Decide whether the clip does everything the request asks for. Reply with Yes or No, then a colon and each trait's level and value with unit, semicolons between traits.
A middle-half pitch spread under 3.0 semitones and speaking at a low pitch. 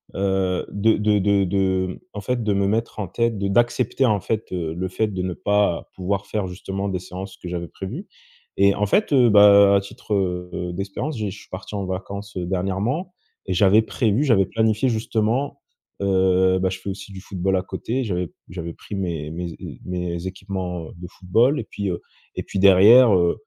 Yes: narrow, 2.5 semitones; very low, 95 Hz